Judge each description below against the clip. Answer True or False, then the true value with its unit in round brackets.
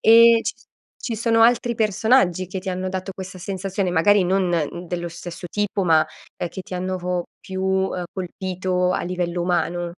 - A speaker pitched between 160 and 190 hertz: True (185 Hz)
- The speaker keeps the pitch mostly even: True (1.9 semitones)